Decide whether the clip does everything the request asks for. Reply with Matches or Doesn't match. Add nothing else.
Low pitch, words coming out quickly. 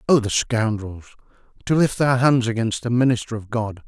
Doesn't match